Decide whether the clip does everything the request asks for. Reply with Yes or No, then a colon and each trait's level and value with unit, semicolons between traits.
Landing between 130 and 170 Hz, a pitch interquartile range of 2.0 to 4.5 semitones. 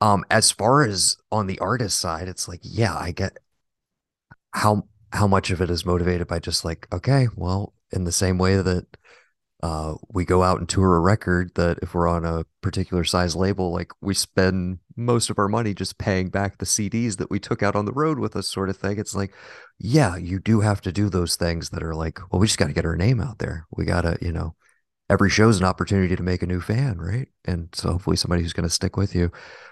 No: very low, 95 Hz; average, 2.8 semitones